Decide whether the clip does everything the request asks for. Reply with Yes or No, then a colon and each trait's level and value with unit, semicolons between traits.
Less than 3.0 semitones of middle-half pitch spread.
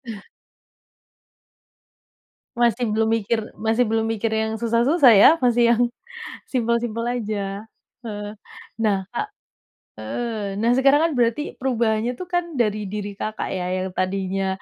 Yes: narrow, 2.6 semitones